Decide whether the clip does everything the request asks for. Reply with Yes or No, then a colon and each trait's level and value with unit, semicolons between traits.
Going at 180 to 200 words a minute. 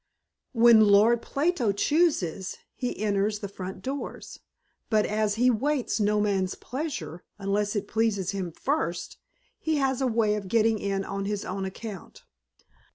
No: average, 150 wpm